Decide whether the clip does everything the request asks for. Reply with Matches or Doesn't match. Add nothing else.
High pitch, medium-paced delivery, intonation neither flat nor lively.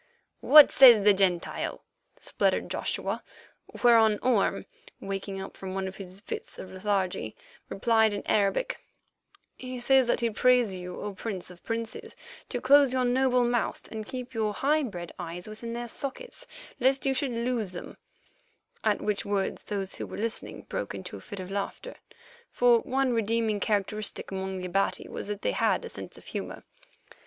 Matches